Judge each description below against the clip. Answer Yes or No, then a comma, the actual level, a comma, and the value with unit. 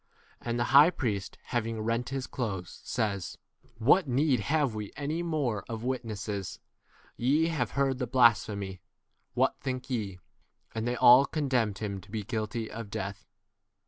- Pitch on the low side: Yes, low, 120 Hz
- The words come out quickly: No, average, 160 wpm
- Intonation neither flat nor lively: Yes, average, 3.9 semitones